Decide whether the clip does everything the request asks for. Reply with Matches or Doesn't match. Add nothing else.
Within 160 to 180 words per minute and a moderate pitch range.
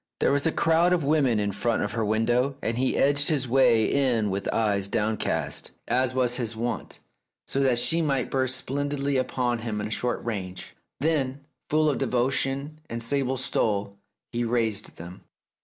Matches